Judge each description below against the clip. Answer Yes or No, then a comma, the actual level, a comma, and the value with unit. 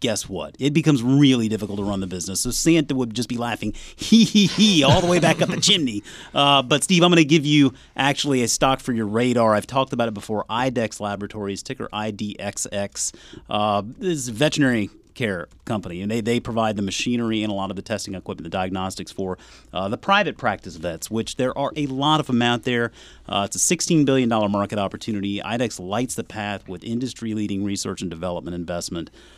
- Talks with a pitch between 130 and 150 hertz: No, low, 115 Hz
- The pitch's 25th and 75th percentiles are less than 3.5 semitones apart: No, average, 5.0 semitones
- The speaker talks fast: Yes, fast, 210 wpm